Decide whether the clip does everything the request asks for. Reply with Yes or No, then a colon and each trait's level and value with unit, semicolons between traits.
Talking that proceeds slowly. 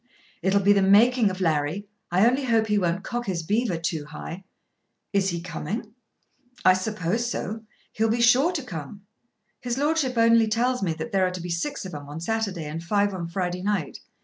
No: average, 200 wpm